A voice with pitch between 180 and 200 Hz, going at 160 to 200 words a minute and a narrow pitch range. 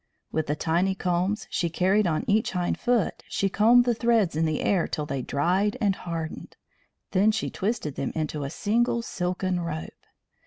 No: medium, 185 Hz; average, 180 wpm; average, 4.6 semitones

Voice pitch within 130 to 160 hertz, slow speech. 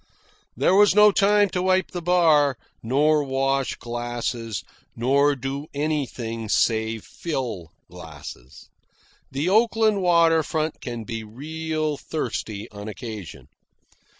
Yes: medium, 140 Hz; slow, 115 wpm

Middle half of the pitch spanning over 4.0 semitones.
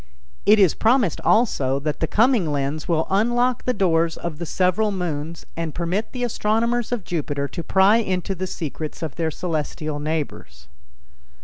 Yes: wide, 5.5 semitones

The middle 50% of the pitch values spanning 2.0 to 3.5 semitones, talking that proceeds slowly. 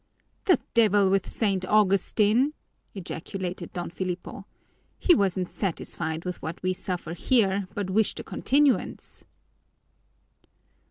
Yes: average, 2.8 semitones; slow, 110 wpm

